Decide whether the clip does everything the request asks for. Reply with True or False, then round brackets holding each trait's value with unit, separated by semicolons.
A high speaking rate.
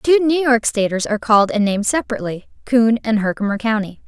False (190 wpm)